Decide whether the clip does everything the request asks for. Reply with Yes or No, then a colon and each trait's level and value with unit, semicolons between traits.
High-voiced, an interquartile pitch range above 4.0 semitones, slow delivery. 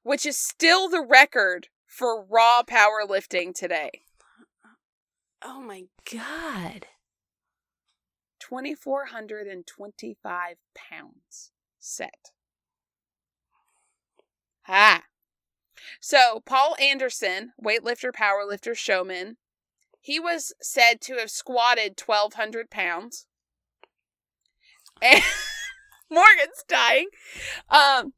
Yes: high, 240 Hz; average, 5.3 semitones; slow, 85 wpm